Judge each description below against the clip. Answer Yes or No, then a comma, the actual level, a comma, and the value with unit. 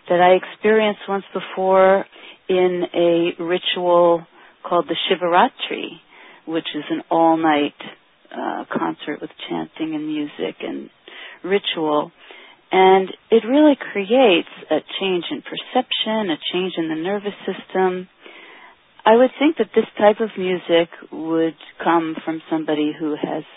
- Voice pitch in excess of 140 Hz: Yes, medium, 185 Hz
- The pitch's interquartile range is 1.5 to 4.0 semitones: No, average, 4.6 semitones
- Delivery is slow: Yes, slow, 130 wpm